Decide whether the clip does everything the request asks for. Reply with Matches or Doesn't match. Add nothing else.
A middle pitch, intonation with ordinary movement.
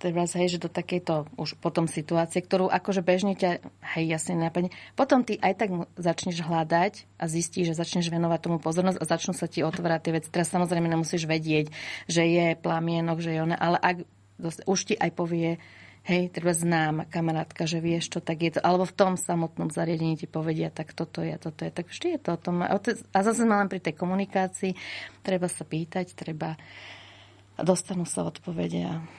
Doesn't match